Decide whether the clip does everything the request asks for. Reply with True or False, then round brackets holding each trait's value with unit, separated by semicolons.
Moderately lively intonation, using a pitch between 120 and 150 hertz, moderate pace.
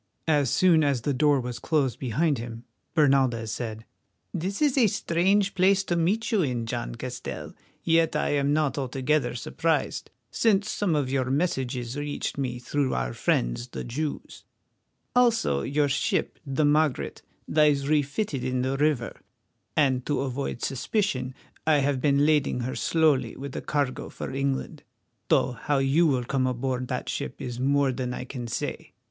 True (3.5 semitones; 140 Hz; 165 wpm)